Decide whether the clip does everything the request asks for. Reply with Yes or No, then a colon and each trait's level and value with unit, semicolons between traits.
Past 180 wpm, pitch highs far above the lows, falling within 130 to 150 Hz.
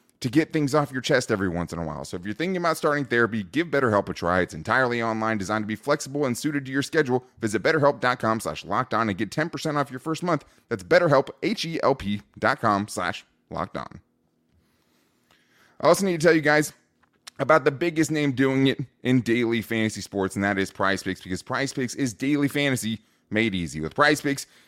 No: average, 200 wpm; wide, 6.3 semitones; low, 120 Hz